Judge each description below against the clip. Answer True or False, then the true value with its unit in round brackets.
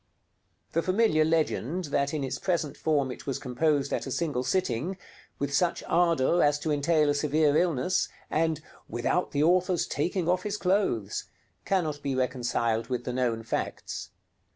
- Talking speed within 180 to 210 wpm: False (160 wpm)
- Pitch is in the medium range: True (150 Hz)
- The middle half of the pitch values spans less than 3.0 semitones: False (4.7 semitones)